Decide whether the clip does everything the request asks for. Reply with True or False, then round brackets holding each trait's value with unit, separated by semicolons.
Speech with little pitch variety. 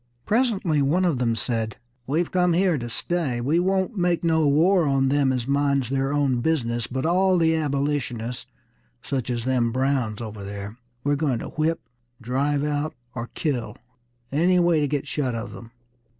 False (4.8 semitones)